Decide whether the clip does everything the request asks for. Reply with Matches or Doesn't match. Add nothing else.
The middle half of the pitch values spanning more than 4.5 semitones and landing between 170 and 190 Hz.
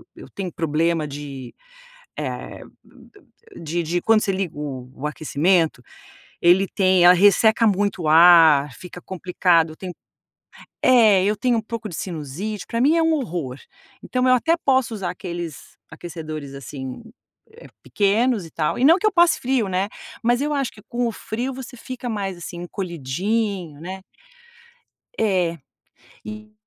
Matches